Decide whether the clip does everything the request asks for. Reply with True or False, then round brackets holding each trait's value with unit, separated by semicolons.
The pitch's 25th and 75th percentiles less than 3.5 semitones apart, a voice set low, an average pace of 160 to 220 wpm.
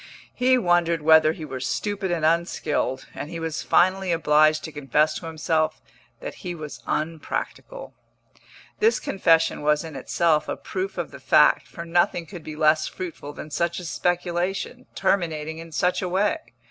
False (2.6 semitones; 165 Hz; 165 wpm)